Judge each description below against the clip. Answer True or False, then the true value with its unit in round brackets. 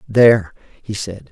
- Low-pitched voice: True (105 Hz)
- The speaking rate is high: False (135 wpm)